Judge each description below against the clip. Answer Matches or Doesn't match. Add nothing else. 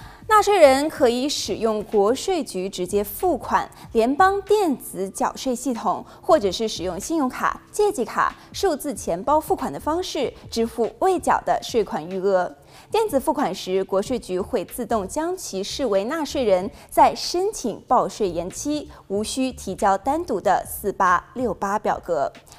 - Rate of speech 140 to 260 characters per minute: Matches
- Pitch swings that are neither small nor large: Doesn't match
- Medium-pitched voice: Doesn't match